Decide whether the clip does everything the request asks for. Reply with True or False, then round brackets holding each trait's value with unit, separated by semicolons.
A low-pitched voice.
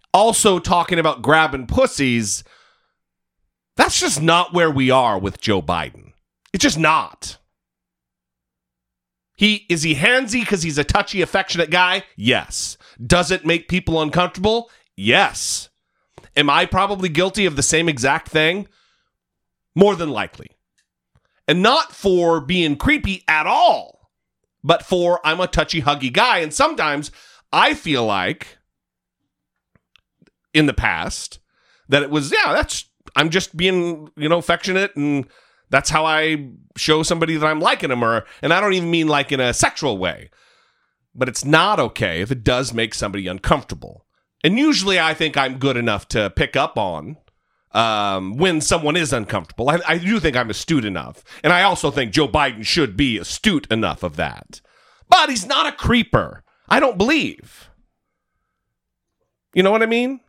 False (155 Hz)